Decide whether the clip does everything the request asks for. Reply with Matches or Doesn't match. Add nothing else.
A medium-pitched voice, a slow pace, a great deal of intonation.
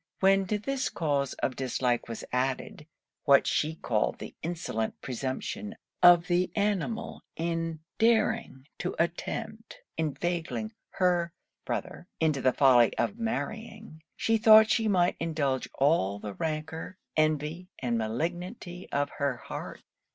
Matches